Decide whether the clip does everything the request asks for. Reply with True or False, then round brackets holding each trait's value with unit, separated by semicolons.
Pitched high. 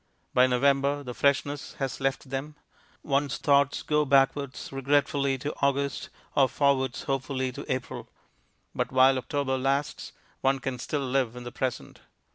False (135 Hz)